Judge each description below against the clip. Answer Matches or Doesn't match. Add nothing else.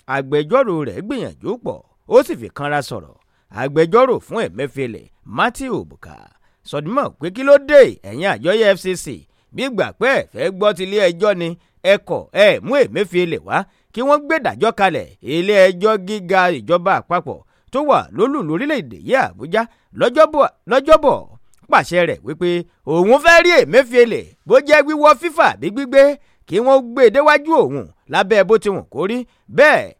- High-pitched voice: Matches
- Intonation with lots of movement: Matches